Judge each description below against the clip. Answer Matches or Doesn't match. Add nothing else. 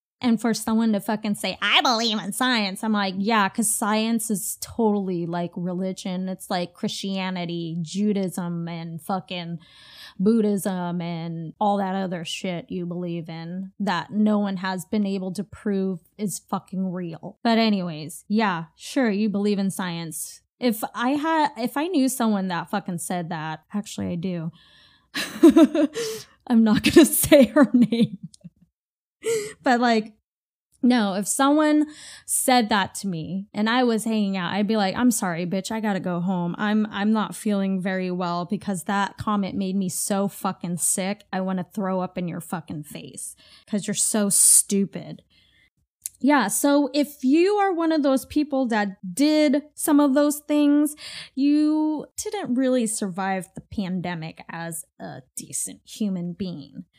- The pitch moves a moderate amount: Matches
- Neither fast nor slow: Matches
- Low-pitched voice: Doesn't match